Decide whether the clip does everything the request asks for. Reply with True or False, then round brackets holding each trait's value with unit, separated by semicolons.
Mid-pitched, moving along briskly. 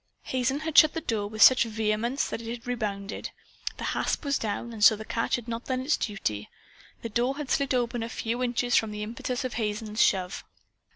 False (230 Hz; 215 wpm)